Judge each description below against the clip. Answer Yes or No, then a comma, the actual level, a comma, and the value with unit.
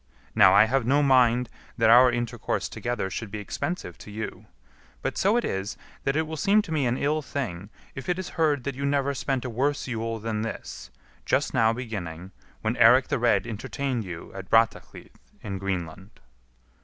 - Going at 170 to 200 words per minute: Yes, average, 190 wpm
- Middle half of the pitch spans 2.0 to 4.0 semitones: No, average, 4.7 semitones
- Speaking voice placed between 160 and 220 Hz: No, low, 120 Hz